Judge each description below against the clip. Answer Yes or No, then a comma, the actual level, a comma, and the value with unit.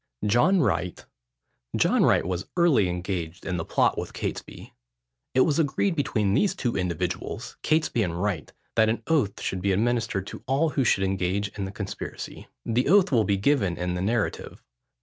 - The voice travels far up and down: Yes, wide, 6.4 semitones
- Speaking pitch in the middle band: No, low, 105 Hz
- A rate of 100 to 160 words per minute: No, average, 175 wpm